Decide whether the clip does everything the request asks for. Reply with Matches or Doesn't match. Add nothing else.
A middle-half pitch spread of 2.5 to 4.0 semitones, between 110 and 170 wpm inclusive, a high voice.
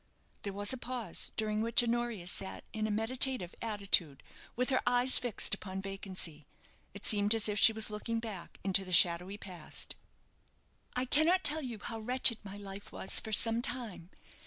Doesn't match